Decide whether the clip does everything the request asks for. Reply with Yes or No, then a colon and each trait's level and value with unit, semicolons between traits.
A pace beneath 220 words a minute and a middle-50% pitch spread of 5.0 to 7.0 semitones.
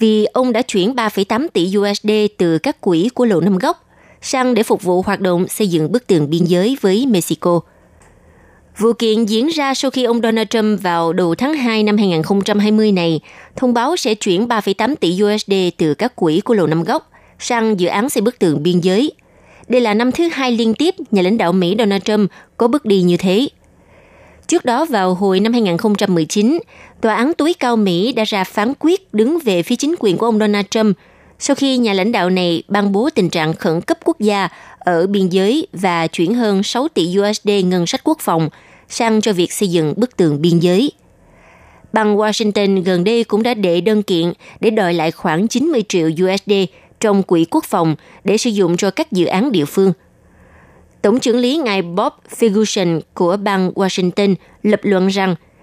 No: average, 200 wpm; average, 4.4 semitones